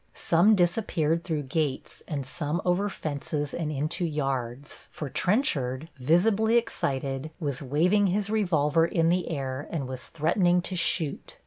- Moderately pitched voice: Yes, medium, 160 Hz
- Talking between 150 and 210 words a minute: No, average, 140 wpm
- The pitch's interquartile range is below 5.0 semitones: Yes, average, 4.1 semitones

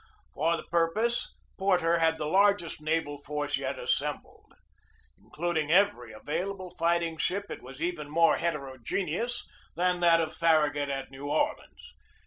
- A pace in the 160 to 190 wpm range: No, slow, 135 wpm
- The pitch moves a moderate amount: Yes, average, 3.3 semitones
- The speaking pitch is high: No, medium, 165 Hz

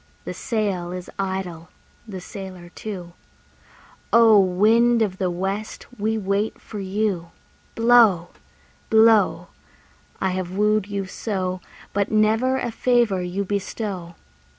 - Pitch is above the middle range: Yes, high, 200 Hz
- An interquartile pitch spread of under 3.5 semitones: Yes, average, 3.0 semitones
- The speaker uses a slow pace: Yes, slow, 120 wpm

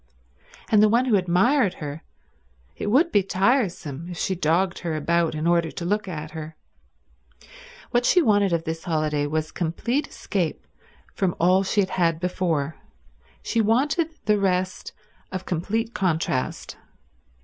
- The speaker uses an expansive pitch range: No, average, 4.5 semitones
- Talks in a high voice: No, medium, 180 Hz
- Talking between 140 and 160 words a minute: Yes, average, 150 wpm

